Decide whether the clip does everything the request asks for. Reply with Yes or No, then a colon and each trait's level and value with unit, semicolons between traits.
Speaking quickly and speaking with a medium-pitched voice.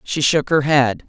Yes: fast, 220 wpm; medium, 145 Hz